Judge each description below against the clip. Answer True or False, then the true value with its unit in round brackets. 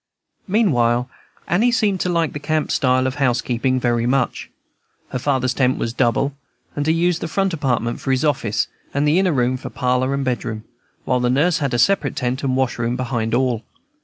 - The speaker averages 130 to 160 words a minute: False (195 wpm)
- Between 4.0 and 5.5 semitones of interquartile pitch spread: False (3.6 semitones)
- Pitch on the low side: True (130 Hz)